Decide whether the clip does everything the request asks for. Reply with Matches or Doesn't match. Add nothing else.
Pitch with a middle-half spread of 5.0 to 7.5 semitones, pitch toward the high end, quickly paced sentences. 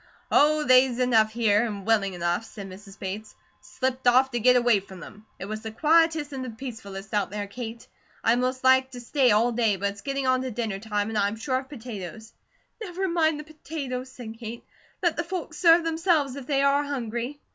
Doesn't match